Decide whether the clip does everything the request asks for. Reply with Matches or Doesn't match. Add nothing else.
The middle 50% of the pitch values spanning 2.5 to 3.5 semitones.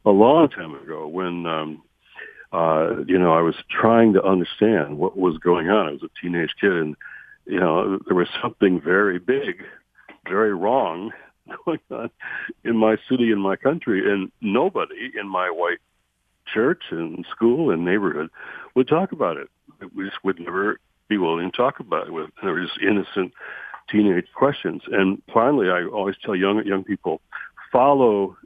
Doesn't match